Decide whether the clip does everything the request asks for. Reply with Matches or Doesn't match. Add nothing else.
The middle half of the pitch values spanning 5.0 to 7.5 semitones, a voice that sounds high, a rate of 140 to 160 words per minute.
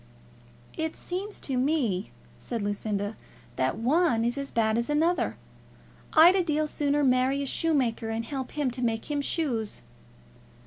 Matches